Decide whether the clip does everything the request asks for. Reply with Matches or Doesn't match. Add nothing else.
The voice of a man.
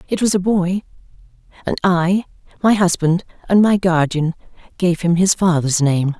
Doesn't match